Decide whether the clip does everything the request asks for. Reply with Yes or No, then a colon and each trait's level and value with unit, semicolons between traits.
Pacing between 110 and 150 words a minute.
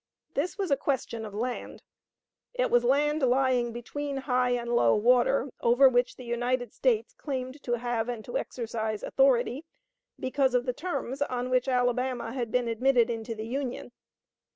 No: average, 165 wpm